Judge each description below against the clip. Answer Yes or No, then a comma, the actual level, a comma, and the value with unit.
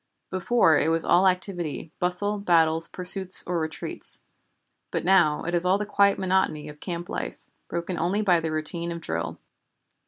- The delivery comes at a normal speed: Yes, average, 165 wpm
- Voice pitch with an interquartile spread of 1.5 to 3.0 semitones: Yes, narrow, 2.6 semitones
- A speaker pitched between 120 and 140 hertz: No, medium, 175 Hz